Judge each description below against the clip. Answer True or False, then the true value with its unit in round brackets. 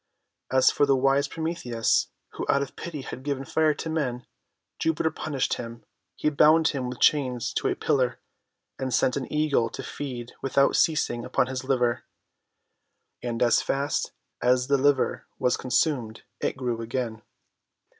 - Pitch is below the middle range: True (130 Hz)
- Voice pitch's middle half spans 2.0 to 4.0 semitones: True (2.8 semitones)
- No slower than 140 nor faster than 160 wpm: True (155 wpm)